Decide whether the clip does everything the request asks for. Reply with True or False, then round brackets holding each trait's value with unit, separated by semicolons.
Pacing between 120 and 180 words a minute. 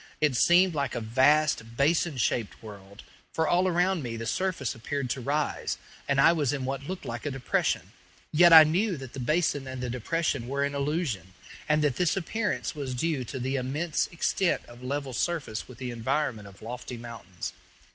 False (190 wpm)